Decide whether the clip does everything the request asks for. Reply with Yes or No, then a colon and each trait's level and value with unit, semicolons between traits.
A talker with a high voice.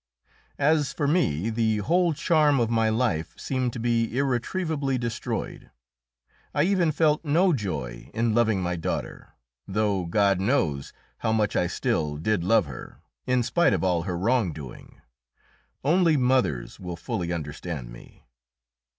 No: low, 115 Hz